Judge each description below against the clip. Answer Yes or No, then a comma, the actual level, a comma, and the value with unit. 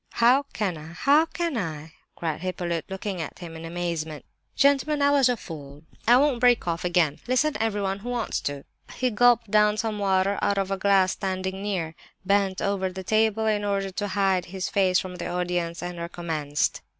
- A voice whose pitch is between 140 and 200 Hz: Yes, high, 190 Hz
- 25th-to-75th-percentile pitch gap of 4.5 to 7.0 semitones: No, average, 4.1 semitones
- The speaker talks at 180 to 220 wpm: Yes, average, 190 wpm